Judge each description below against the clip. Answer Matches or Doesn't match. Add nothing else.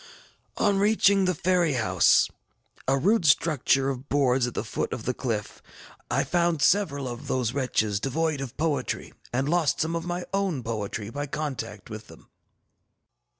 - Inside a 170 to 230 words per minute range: Doesn't match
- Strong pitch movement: Matches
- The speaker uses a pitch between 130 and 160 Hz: Matches